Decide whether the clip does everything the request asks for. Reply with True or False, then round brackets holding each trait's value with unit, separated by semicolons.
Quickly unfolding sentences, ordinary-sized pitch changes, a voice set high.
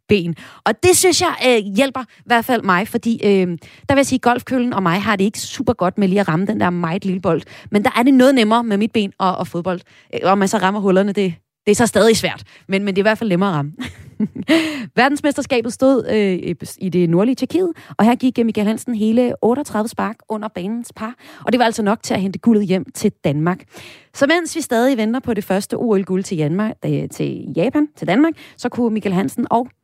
True (230 wpm; 4.5 semitones; 220 Hz)